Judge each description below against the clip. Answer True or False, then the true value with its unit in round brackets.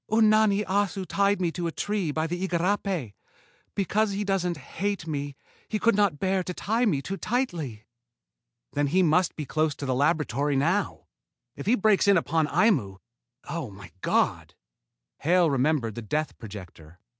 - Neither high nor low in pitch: True (170 Hz)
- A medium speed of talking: True (165 wpm)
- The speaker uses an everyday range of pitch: False (5.7 semitones)